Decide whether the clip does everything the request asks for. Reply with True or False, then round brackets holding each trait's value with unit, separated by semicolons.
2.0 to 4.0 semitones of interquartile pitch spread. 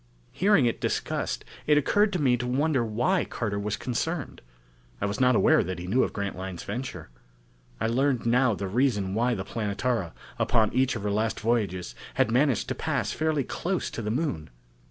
False (4.8 semitones)